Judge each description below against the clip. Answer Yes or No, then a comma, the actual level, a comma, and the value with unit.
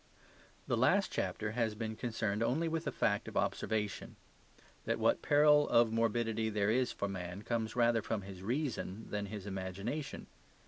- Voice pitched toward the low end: Yes, low, 110 Hz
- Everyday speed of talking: Yes, average, 165 wpm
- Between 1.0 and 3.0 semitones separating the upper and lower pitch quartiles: Yes, narrow, 2.6 semitones